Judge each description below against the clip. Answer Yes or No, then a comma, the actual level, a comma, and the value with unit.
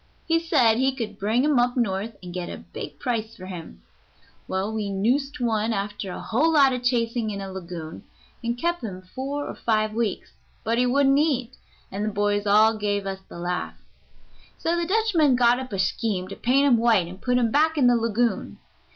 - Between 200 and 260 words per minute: Yes, fast, 205 wpm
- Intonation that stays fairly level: No, average, 4.5 semitones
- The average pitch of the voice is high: Yes, high, 230 Hz